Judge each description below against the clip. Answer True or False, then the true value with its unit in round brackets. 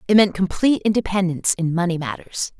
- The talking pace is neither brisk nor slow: True (160 wpm)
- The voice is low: False (185 Hz)